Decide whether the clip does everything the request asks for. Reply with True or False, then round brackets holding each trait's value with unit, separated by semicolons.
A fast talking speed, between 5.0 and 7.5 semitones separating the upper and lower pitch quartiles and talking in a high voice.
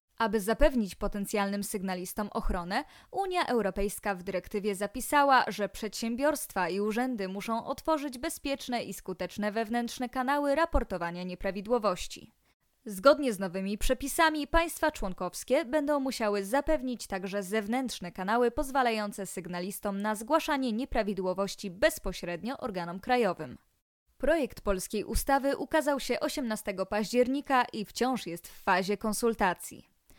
False (110 wpm; 5.3 semitones; 225 Hz)